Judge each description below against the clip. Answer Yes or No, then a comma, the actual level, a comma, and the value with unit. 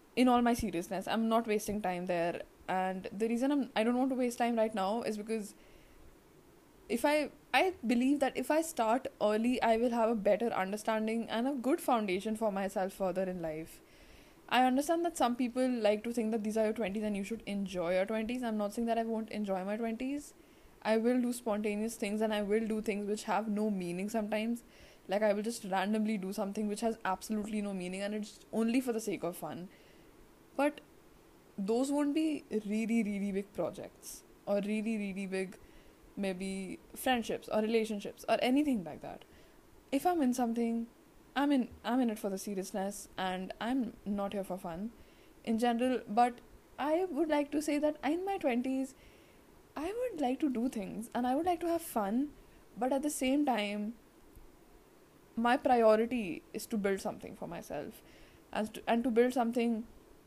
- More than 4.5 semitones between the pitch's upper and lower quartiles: No, average, 3.4 semitones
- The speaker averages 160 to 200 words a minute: Yes, average, 190 wpm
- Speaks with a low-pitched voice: No, high, 225 Hz